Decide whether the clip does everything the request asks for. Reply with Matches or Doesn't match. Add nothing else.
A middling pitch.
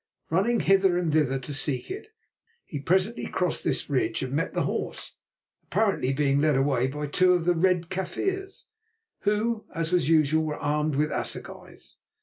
Matches